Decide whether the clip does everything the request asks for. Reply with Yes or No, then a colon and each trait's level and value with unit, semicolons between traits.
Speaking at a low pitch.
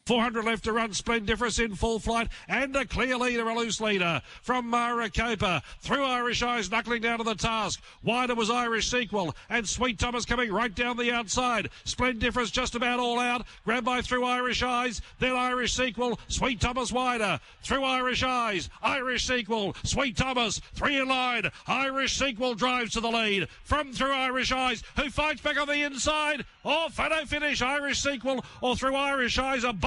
No: high, 245 Hz